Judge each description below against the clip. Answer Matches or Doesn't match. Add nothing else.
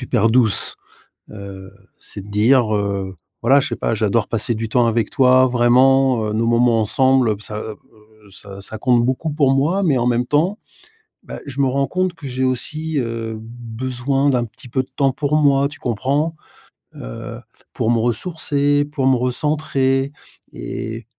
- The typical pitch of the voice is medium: Doesn't match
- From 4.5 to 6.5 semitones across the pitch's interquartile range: Doesn't match